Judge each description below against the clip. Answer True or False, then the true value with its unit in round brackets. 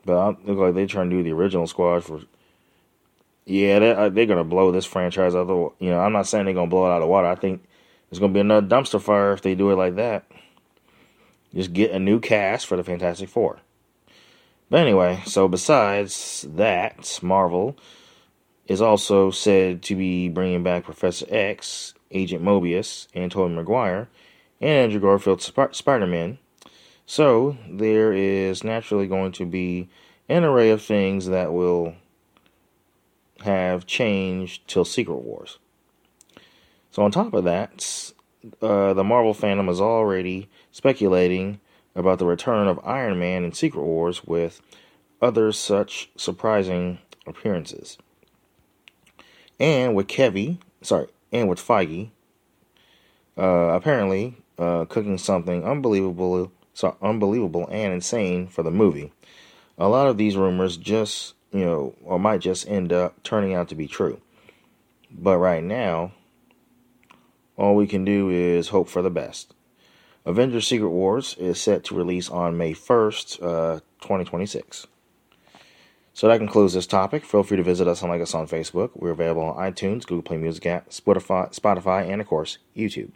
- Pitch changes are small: True (2.3 semitones)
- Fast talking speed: False (160 wpm)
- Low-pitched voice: True (95 Hz)